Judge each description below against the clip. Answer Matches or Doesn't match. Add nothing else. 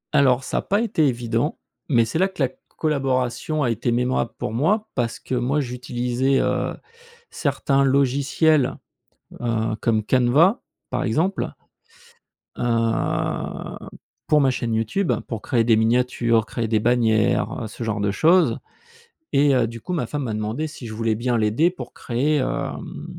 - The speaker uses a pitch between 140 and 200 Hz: Doesn't match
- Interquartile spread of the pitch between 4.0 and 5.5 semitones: Doesn't match